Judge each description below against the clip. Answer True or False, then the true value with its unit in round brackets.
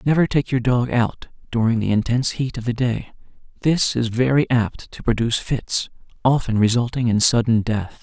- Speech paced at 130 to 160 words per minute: False (180 wpm)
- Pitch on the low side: True (120 Hz)